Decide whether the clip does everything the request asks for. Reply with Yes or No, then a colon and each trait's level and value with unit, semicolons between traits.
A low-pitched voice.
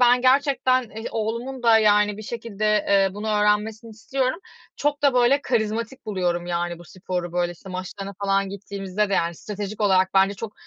No: high, 210 Hz